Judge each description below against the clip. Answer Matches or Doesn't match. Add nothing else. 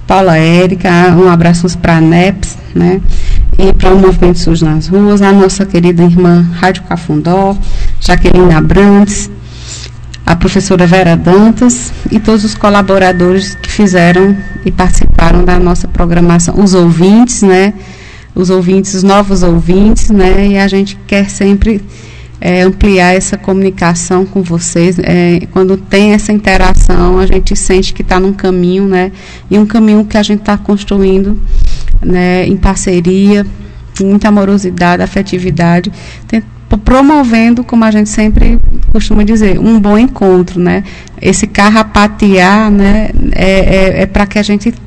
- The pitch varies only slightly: Matches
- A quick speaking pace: Doesn't match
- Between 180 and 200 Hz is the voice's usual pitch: Matches